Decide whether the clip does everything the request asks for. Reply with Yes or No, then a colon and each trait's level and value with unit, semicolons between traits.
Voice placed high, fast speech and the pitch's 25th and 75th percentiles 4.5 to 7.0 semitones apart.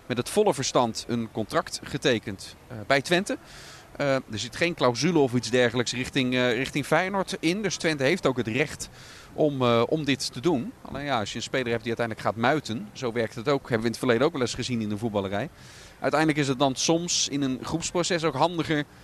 No: low, 130 Hz; fast, 215 wpm; average, 4.8 semitones